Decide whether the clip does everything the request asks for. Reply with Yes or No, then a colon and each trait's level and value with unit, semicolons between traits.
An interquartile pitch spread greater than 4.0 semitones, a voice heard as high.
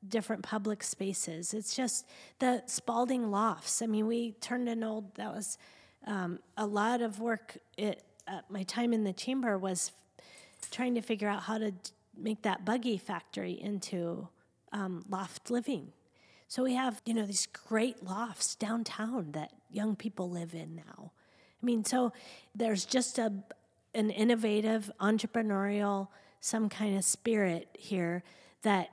No: average, 2.9 semitones; high, 215 Hz